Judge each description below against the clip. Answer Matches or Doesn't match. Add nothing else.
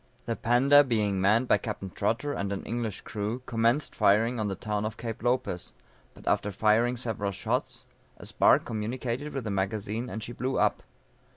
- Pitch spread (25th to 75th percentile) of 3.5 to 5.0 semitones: Doesn't match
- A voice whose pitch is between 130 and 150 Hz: Doesn't match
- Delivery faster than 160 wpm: Matches